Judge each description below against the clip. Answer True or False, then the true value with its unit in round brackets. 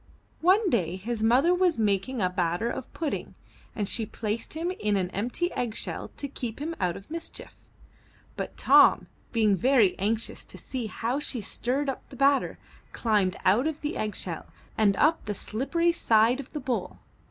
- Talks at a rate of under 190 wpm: True (175 wpm)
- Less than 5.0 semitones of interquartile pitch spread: False (5.6 semitones)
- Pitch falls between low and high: False (235 Hz)